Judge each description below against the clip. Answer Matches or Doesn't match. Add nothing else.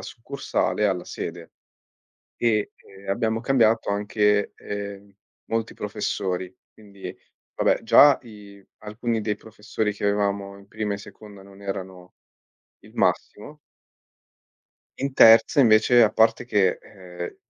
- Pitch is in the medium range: Doesn't match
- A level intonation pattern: Matches